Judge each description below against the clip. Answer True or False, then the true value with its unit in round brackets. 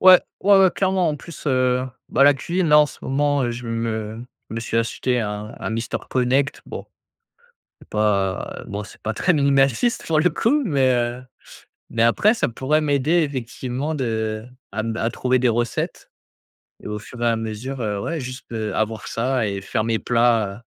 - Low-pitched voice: True (125 Hz)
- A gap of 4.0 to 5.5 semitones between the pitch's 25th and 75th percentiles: True (4.3 semitones)